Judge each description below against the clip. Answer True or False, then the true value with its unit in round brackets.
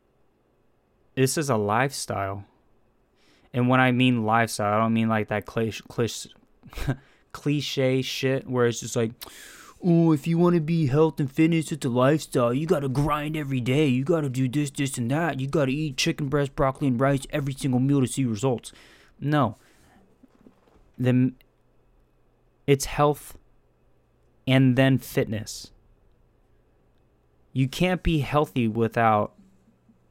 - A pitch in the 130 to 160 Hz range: True (135 Hz)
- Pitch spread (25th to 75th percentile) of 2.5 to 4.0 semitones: True (3.7 semitones)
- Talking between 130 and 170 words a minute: True (145 wpm)